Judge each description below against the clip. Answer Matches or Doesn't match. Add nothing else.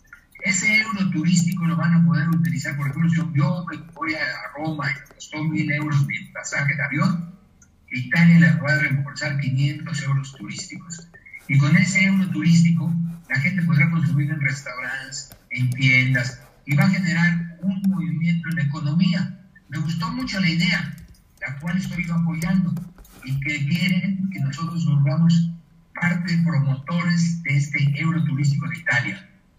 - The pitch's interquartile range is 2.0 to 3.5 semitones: Matches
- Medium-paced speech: Matches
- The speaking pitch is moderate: Matches